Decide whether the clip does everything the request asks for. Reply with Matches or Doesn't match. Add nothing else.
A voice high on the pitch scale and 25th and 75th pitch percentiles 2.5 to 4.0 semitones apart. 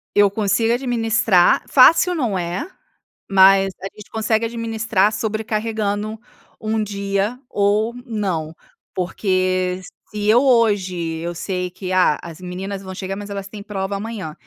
Matches